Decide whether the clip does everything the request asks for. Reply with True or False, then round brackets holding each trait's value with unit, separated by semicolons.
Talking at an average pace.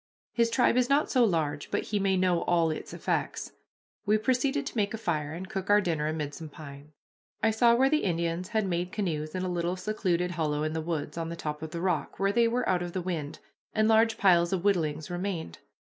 False (230 wpm)